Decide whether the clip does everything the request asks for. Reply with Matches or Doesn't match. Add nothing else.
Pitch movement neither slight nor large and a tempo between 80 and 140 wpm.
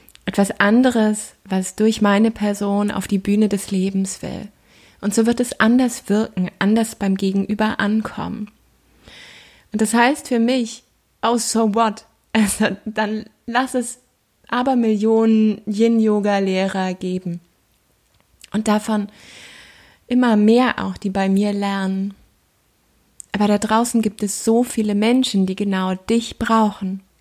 Doesn't match